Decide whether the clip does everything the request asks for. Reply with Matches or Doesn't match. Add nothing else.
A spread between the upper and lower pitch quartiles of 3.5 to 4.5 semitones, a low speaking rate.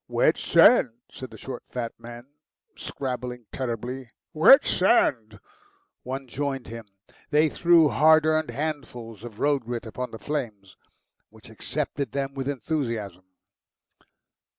Matches